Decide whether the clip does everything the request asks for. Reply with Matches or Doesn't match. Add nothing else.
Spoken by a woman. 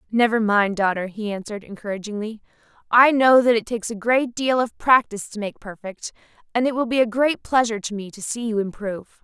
Matches